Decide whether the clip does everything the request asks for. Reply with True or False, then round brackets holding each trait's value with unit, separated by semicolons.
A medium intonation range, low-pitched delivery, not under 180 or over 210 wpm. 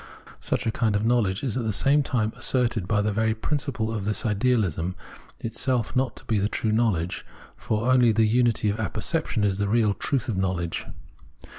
True (3.0 semitones; 110 Hz; 185 wpm)